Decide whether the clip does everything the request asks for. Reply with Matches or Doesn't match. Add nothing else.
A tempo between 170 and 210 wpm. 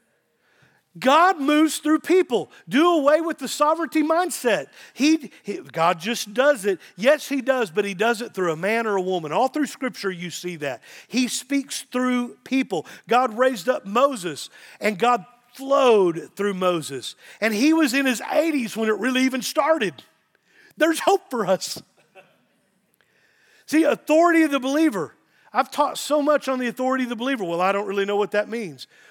Matches